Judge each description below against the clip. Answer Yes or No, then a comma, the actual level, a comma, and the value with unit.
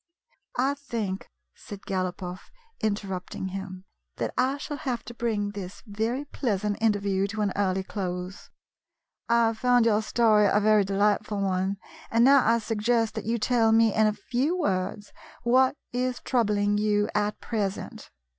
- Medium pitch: No, high, 210 Hz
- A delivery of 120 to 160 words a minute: Yes, average, 155 wpm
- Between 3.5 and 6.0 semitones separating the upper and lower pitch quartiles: No, average, 2.9 semitones